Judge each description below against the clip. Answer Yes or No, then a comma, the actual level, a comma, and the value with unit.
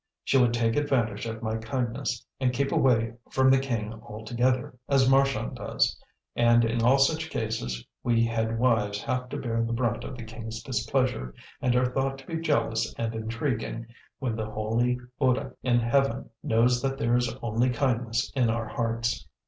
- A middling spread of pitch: No, narrow, 2.3 semitones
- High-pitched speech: No, low, 120 Hz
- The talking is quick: No, average, 175 wpm